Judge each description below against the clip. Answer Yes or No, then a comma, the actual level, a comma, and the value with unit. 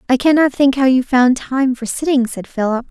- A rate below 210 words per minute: No, fast, 225 wpm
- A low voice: No, very high, 260 Hz